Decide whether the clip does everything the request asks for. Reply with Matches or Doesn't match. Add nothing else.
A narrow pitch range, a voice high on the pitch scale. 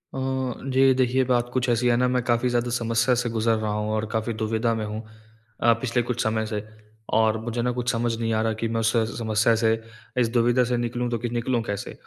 Doesn't match